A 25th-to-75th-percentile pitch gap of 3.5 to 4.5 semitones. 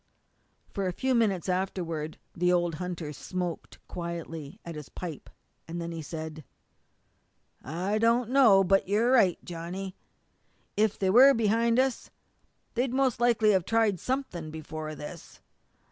No: wide, 5.4 semitones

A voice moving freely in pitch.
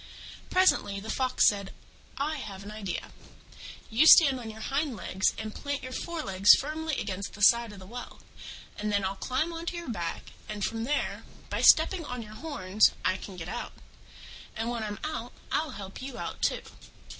Yes: wide, 6.0 semitones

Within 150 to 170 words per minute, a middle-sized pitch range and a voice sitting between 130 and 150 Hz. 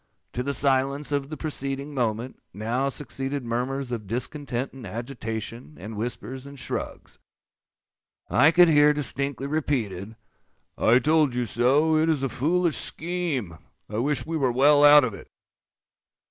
No: average, 140 wpm; average, 3.5 semitones; low, 135 Hz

